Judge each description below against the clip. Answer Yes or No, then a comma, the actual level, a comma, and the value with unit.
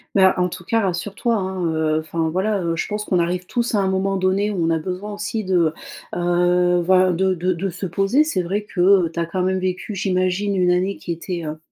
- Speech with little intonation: Yes, narrow, 2.0 semitones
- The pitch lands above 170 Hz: Yes, medium, 185 Hz